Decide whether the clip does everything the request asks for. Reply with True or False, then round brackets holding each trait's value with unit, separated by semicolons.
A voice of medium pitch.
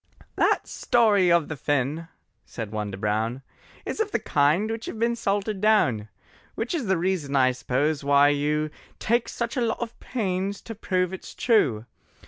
True (175 Hz)